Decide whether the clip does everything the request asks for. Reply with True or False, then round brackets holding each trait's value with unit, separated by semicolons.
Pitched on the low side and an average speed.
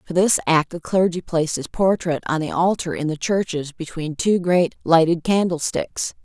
False (170 Hz; 190 wpm)